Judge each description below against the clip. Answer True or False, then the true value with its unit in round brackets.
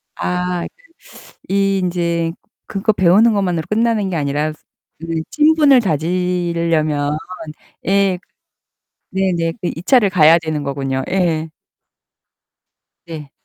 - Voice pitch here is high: False (175 Hz)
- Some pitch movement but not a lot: True (3.5 semitones)